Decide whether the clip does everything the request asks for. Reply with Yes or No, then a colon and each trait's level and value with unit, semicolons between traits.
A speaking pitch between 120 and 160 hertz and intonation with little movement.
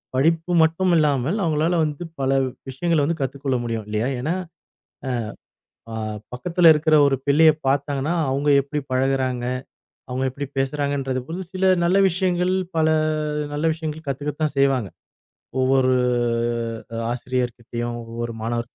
No: medium, 140 Hz; average, 3.8 semitones